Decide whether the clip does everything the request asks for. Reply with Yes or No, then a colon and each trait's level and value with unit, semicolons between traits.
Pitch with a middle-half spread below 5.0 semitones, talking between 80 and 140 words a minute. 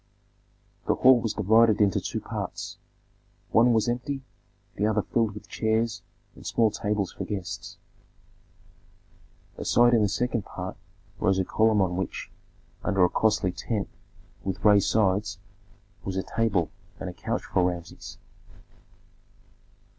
Yes: average, 2.9 semitones; slow, 135 wpm